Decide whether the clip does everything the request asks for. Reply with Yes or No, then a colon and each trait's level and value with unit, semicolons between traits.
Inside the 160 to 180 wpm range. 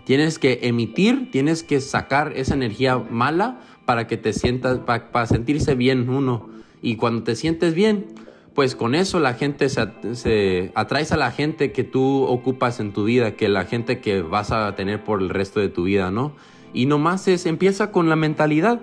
No: average, 195 wpm